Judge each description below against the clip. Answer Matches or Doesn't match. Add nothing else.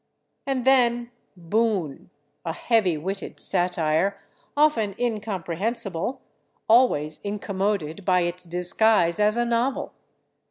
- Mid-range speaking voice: Doesn't match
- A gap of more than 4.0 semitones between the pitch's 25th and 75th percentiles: Matches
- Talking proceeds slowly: Matches